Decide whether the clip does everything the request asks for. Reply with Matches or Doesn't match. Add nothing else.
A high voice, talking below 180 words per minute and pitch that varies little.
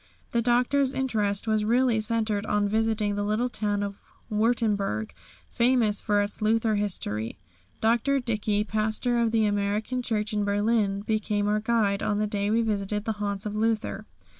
Matches